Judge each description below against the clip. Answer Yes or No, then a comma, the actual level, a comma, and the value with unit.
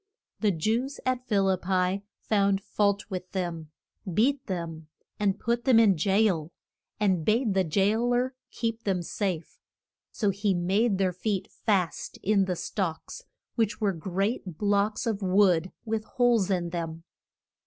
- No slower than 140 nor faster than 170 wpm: Yes, average, 150 wpm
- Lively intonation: No, average, 3.3 semitones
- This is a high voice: Yes, high, 195 Hz